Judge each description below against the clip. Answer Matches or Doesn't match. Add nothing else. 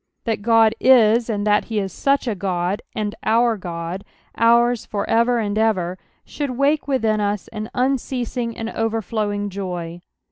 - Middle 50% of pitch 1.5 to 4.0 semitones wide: Matches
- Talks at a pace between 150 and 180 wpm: Matches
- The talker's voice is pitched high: Matches